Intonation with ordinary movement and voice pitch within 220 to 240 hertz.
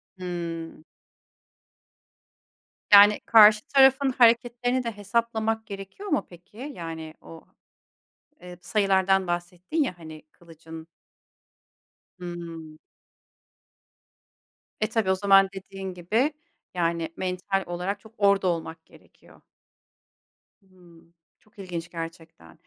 No: average, 4.0 semitones; medium, 185 Hz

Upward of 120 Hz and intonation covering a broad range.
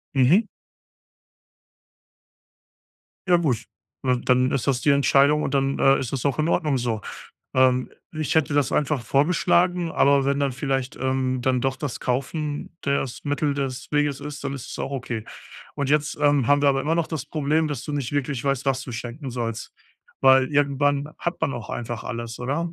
No: medium, 140 Hz; narrow, 2.4 semitones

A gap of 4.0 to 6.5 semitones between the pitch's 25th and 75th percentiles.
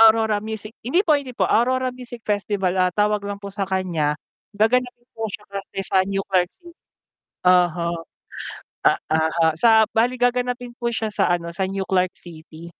Yes: average, 4.5 semitones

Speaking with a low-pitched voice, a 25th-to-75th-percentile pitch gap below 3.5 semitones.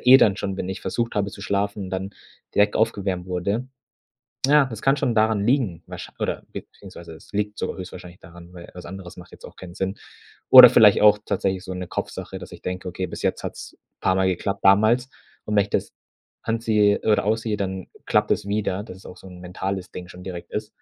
Yes: very low, 95 Hz; narrow, 2.5 semitones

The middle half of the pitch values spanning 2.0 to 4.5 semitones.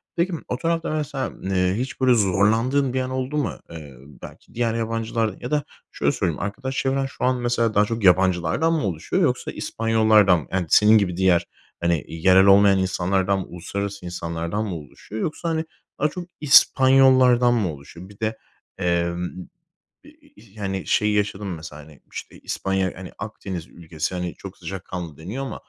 No: wide, 5.6 semitones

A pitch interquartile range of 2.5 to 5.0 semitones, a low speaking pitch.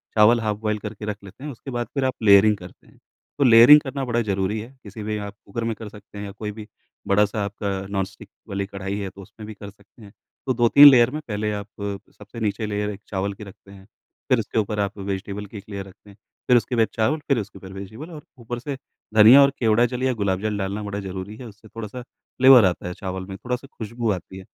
Yes: average, 2.9 semitones; low, 105 Hz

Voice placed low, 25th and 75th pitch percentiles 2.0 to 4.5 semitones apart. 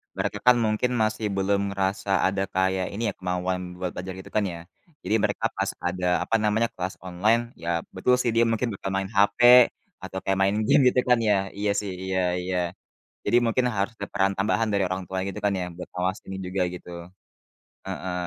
Yes: very low, 95 Hz; narrow, 2.6 semitones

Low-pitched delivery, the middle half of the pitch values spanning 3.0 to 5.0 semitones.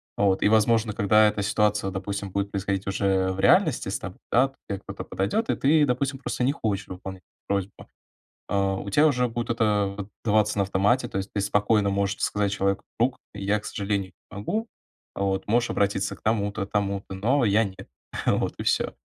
No: low, 100 Hz; narrow, 2.4 semitones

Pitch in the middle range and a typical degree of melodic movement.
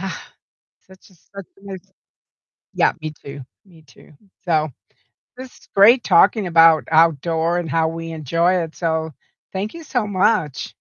Yes: medium, 170 Hz; average, 3.3 semitones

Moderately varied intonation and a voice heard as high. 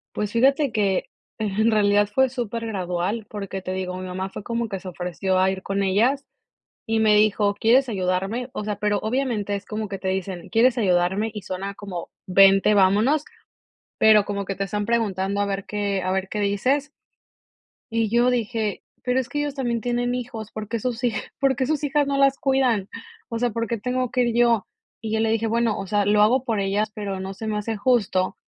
Yes: average, 3.3 semitones; high, 210 Hz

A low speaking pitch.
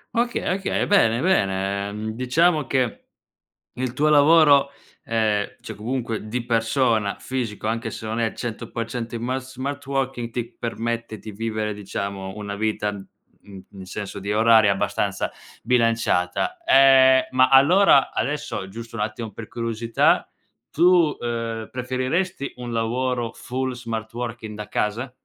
Yes: low, 115 Hz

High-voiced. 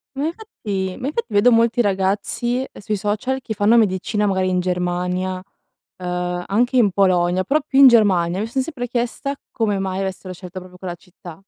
Yes: high, 200 Hz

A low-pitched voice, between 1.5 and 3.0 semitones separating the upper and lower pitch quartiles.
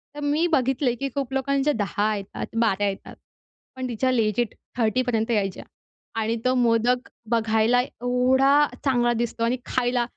No: high, 245 Hz; average, 2.7 semitones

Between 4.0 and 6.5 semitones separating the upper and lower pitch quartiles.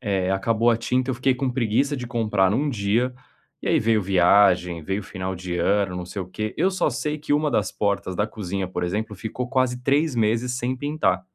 Yes: average, 4.8 semitones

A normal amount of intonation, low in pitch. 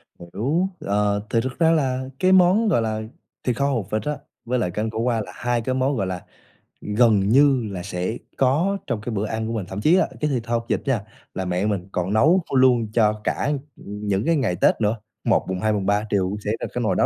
Yes: average, 4.2 semitones; low, 115 Hz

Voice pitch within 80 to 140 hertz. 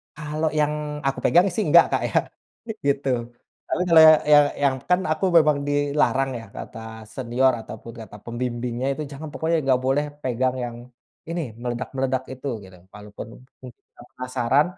Yes: low, 135 Hz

